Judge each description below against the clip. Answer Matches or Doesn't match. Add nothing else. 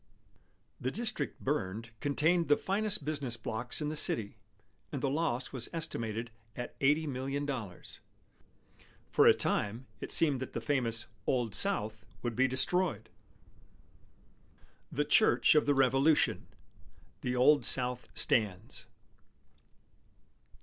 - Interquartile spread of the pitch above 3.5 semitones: Matches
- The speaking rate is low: Matches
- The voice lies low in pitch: Matches